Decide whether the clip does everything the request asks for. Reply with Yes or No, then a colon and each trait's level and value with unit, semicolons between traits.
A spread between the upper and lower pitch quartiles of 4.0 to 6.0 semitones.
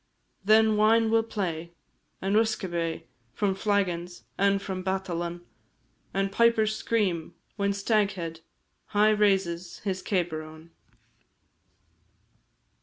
No: average, 3.6 semitones